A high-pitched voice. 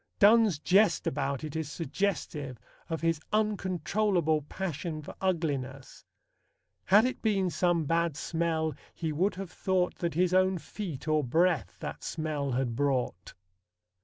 No: medium, 165 Hz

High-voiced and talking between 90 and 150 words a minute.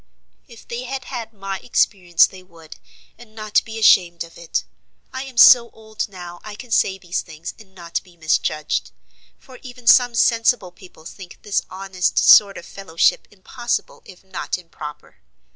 No: high, 195 Hz; average, 165 wpm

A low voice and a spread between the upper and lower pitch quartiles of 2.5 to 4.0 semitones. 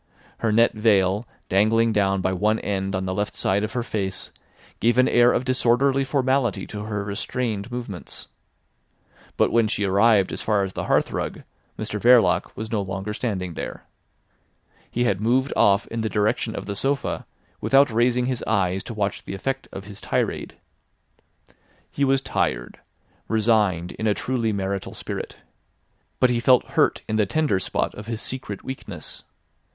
Yes: low, 110 Hz; average, 3.6 semitones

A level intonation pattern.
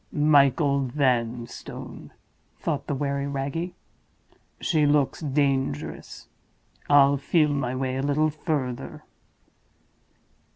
Yes: narrow, 1.9 semitones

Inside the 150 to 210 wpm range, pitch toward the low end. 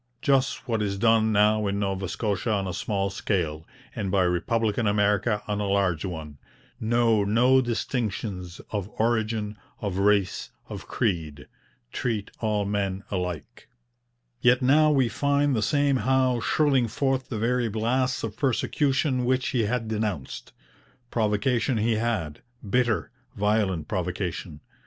No: average, 140 wpm; low, 110 Hz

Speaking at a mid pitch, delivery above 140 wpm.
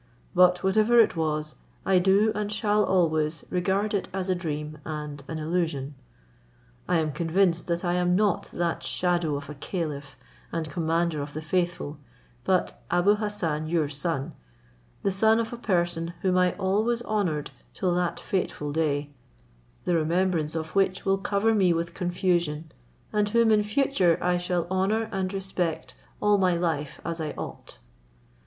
Yes: medium, 175 Hz; average, 160 wpm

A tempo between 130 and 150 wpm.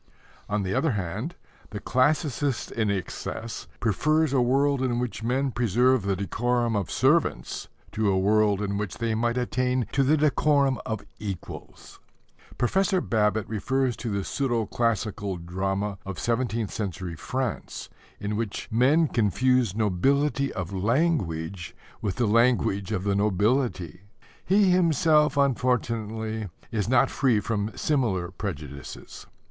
Yes: slow, 135 wpm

